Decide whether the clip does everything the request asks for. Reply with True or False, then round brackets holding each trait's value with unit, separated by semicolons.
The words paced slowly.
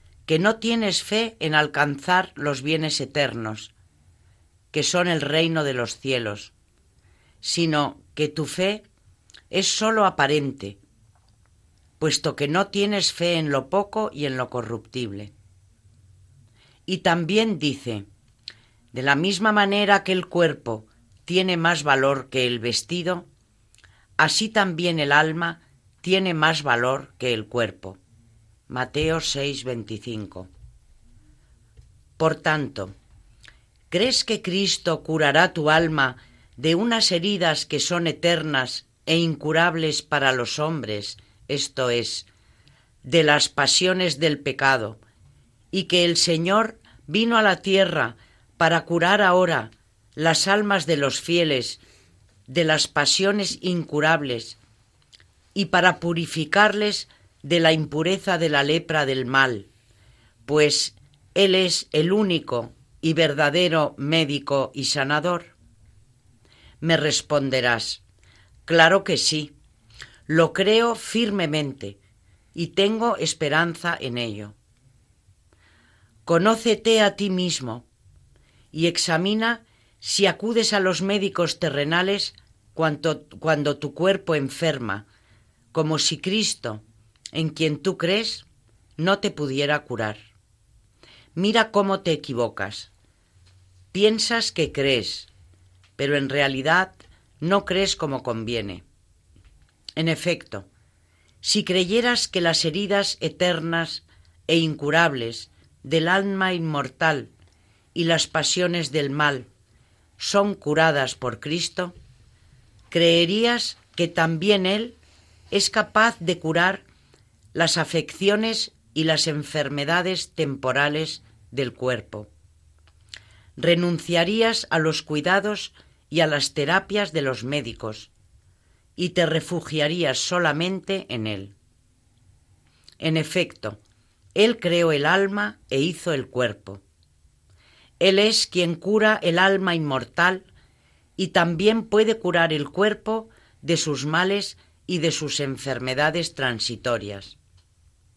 True (110 wpm)